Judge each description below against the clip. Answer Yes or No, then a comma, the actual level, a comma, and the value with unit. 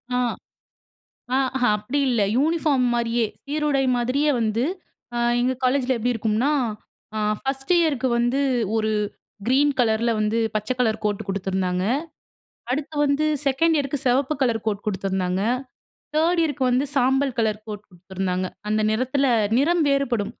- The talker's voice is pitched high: Yes, high, 245 Hz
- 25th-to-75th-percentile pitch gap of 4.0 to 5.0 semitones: Yes, average, 4.6 semitones